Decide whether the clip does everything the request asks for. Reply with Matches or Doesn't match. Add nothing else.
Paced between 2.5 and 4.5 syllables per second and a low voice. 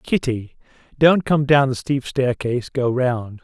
Matches